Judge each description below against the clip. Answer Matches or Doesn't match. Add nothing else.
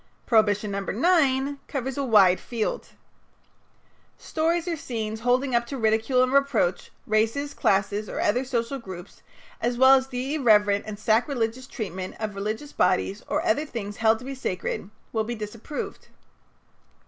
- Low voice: Doesn't match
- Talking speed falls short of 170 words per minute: Matches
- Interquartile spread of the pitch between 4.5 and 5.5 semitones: Doesn't match